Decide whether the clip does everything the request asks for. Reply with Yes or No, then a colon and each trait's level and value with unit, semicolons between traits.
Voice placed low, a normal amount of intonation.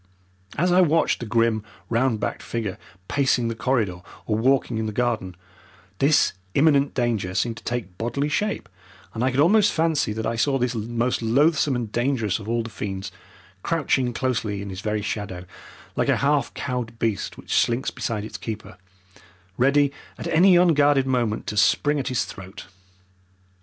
Yes: low, 120 Hz; average, 4.4 semitones